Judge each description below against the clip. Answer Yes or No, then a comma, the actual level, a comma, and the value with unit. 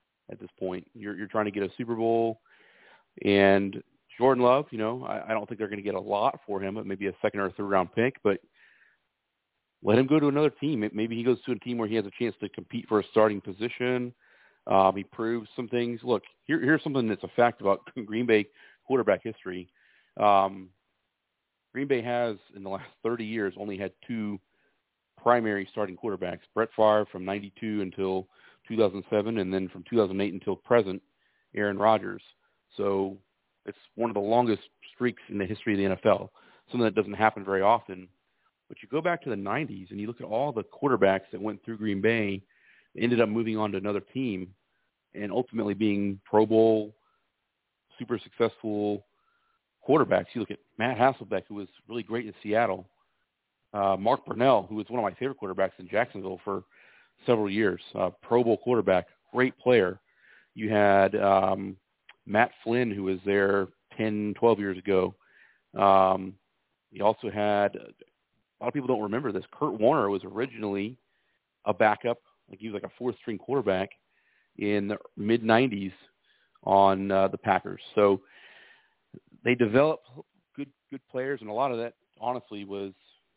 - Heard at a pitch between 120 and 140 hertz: No, low, 105 Hz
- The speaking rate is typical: Yes, average, 180 wpm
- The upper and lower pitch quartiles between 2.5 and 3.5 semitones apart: Yes, average, 3.1 semitones